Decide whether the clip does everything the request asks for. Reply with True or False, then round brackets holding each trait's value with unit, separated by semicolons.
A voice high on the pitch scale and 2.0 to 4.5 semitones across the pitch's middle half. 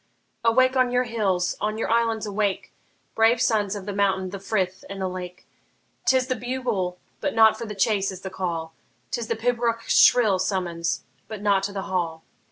True (205 Hz; 3.5 semitones)